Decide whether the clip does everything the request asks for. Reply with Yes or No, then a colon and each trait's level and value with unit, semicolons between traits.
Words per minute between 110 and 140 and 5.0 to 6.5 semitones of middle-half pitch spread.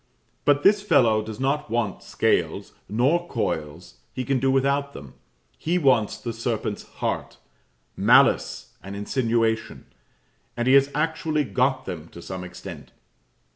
Yes: slow, 135 wpm; average, 5.3 semitones